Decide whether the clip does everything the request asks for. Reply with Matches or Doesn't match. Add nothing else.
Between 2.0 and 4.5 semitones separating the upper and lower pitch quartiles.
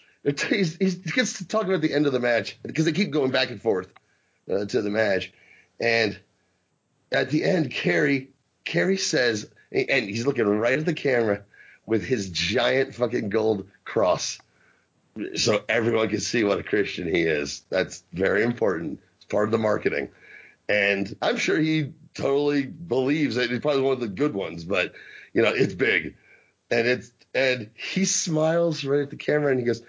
Doesn't match